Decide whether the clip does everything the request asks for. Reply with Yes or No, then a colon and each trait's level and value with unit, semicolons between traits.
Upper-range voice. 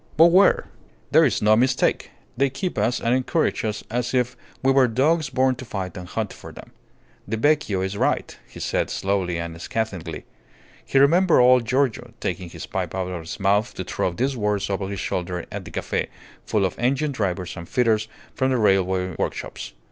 No: low, 110 Hz